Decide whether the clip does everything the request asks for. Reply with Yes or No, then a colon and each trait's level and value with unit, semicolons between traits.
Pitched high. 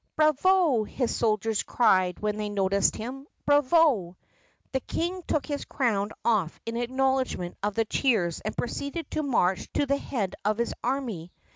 Yes: high, 235 Hz